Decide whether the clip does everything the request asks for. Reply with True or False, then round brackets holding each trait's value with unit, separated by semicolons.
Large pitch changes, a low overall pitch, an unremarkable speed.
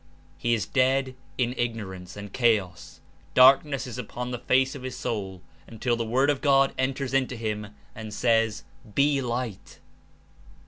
False (3.2 semitones; 120 Hz; 150 wpm)